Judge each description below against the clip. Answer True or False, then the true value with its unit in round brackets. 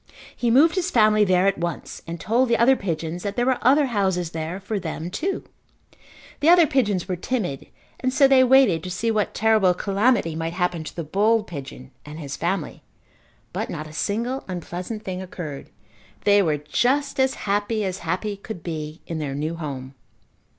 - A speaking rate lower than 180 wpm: False (185 wpm)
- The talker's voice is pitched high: True (195 Hz)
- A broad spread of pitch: True (5.9 semitones)